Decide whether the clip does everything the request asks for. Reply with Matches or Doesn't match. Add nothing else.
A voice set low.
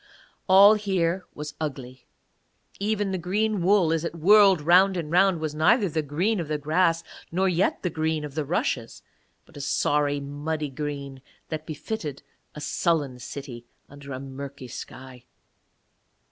Doesn't match